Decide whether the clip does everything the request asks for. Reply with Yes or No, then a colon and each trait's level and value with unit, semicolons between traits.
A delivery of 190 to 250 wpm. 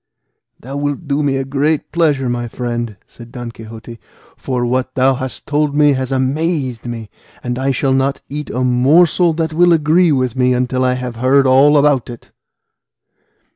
No: average, 175 wpm